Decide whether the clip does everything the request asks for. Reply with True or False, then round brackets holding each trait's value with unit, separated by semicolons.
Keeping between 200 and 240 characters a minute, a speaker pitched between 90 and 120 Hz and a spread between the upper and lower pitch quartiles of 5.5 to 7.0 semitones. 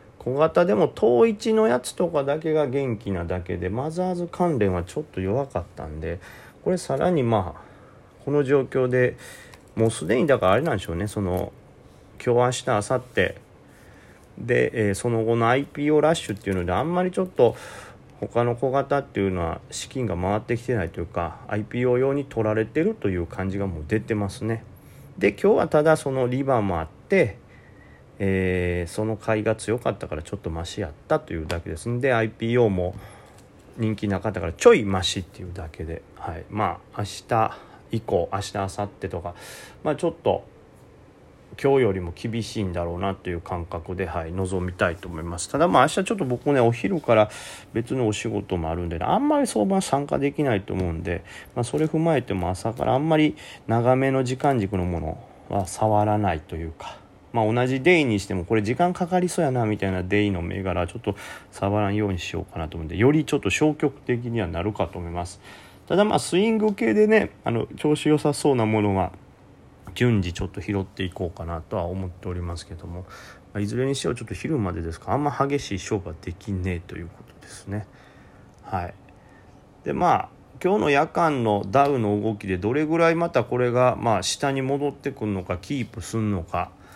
False (380 characters per minute; 105 Hz; 6.2 semitones)